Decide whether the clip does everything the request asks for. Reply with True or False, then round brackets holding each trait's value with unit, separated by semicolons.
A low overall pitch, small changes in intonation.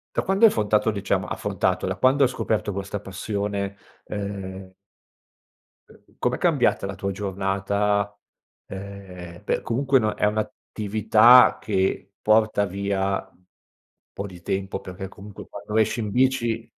True (100 Hz; 1.9 semitones)